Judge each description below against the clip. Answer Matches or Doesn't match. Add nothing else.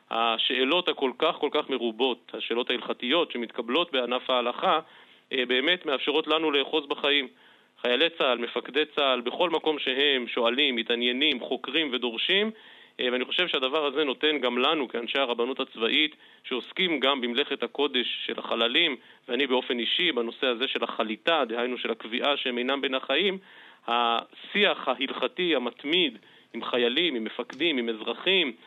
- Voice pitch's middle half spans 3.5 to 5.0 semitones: Matches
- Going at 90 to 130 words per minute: Doesn't match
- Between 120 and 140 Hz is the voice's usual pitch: Matches